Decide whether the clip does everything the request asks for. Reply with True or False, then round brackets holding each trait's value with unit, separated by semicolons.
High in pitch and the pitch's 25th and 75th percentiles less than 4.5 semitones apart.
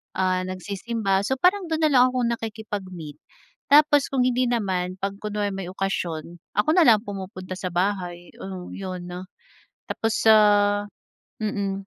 True (200 Hz; 4.1 semitones)